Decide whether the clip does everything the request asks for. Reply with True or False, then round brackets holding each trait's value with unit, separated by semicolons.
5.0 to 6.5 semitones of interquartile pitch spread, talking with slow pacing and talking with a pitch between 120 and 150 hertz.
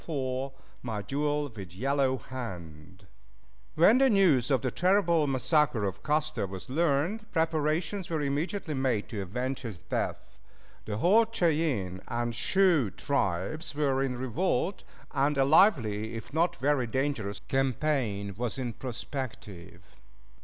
True (5.6 semitones; 130 wpm; 135 Hz)